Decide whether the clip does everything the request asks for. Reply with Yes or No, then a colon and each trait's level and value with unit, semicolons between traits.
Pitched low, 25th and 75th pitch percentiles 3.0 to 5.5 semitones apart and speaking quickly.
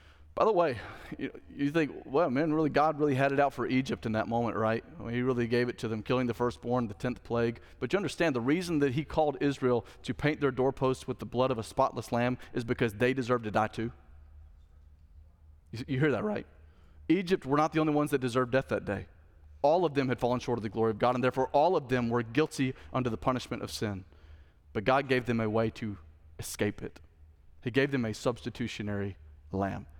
Yes: low, 120 Hz; average, 4.6 semitones; fast, 225 wpm